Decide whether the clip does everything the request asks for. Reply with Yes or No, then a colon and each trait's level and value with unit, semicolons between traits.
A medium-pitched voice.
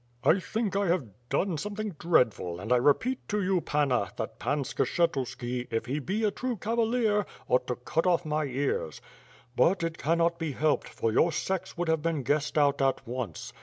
Yes: medium, 155 Hz